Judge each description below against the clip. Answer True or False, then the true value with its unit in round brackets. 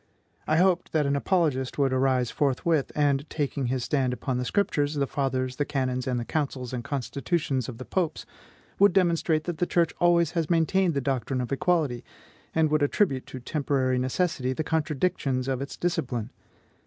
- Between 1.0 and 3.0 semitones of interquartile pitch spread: False (4.0 semitones)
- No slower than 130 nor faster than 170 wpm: False (180 wpm)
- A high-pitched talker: False (140 Hz)